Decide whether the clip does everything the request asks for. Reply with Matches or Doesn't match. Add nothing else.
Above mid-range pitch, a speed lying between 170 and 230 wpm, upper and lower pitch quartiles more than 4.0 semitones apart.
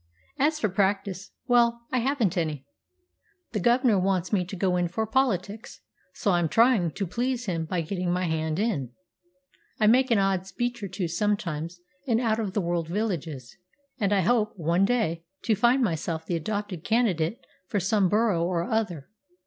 Matches